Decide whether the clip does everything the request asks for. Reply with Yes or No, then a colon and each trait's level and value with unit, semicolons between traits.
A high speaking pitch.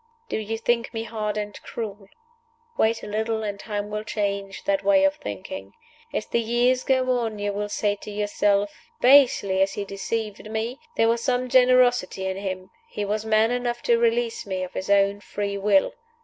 Yes: high, 215 Hz